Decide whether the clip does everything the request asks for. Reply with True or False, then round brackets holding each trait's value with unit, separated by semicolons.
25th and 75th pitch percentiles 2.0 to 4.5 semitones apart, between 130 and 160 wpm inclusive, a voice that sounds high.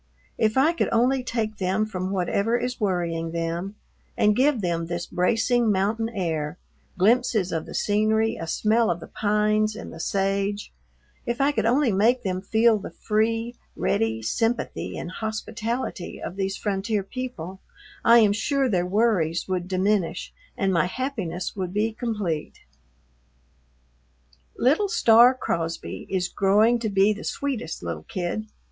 True (4.0 semitones; 150 wpm; 210 Hz)